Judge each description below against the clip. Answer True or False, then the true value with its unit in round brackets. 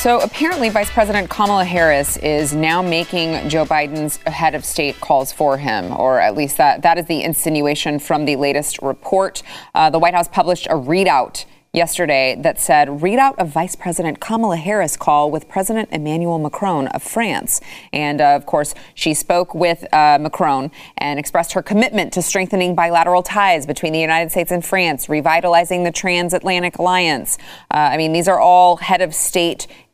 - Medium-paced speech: True (175 wpm)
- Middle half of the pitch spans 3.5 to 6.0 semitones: False (3.1 semitones)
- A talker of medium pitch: True (170 Hz)